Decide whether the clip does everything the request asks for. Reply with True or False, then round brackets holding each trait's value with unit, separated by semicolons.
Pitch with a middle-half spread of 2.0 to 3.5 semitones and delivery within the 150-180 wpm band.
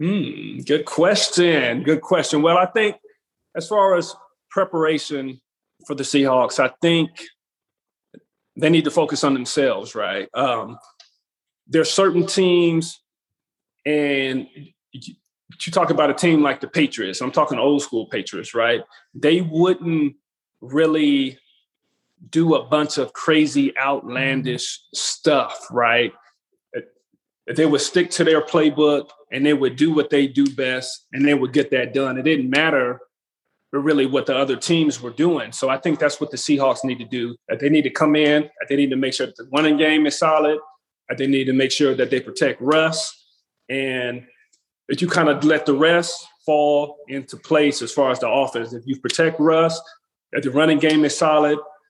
True (3.0 semitones; 175 wpm)